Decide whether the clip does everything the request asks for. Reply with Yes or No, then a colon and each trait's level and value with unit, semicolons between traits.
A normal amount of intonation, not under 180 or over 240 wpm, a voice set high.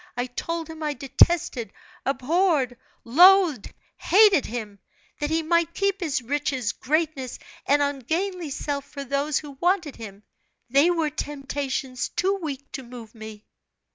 No: average, 4.6 semitones; average, 140 wpm; very high, 285 Hz